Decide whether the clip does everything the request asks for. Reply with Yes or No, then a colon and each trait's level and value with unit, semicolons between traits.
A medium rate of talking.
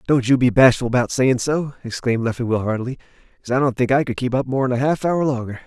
No: fast, 245 wpm